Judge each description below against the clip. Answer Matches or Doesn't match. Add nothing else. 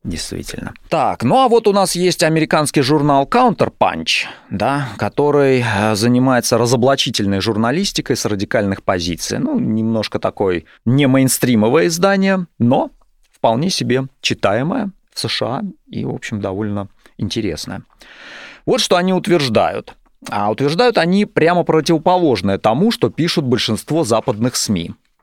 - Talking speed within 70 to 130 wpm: Matches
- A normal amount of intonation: Doesn't match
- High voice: Doesn't match